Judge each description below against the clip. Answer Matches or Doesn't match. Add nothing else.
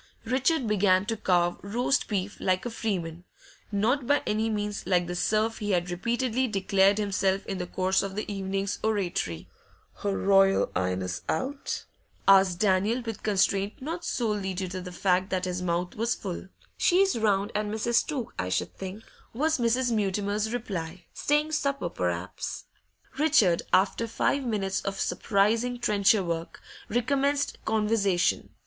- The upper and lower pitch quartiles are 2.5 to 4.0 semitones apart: Matches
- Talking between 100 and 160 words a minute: Matches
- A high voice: Matches